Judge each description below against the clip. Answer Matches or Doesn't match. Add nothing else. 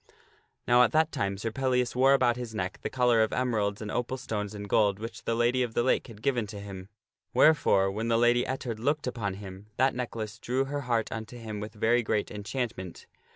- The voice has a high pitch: Doesn't match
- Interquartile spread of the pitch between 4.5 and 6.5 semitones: Doesn't match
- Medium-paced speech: Doesn't match